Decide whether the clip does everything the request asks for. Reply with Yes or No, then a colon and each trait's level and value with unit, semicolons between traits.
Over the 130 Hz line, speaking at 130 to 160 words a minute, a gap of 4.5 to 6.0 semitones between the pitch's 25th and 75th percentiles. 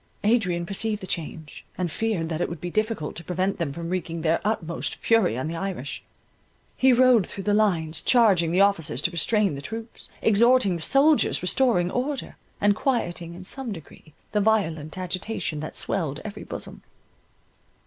No: medium, 185 Hz; average, 170 wpm; average, 4.9 semitones